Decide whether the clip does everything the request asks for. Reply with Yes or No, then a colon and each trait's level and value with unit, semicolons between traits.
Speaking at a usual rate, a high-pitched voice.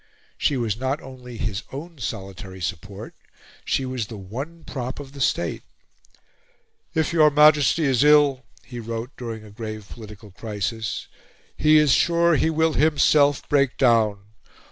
No: average, 145 wpm; low, 125 Hz